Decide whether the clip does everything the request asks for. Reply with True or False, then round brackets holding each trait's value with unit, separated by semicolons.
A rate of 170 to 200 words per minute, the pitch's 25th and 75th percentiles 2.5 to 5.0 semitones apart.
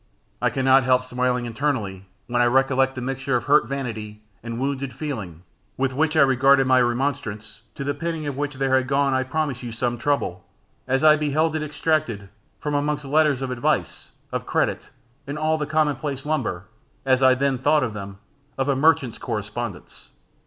True (180 wpm; 3.0 semitones)